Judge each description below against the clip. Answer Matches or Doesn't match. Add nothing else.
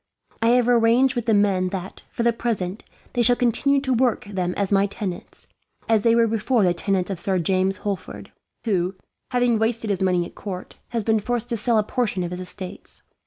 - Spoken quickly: Matches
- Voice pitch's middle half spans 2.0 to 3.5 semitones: Doesn't match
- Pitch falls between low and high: Doesn't match